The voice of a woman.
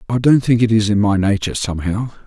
No: male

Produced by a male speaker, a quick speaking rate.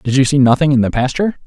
Yes: male; fast, 285 wpm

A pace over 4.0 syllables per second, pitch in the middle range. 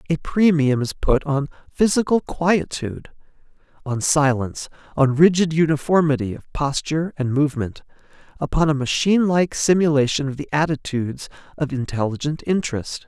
Yes: 5.3 syllables/s; medium, 150 Hz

